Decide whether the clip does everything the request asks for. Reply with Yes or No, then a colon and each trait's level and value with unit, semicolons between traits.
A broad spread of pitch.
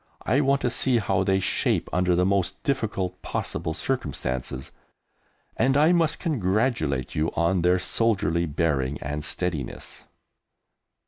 Yes: wide, 7.4 semitones